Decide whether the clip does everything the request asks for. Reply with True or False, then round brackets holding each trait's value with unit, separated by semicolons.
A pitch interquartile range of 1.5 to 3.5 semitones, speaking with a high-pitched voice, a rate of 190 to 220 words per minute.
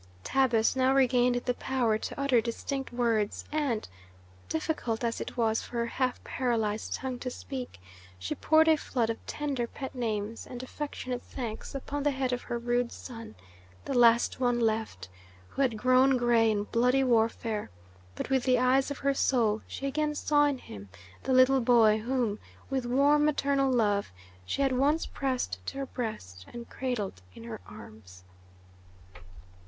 False (3.1 semitones; 245 Hz; 165 wpm)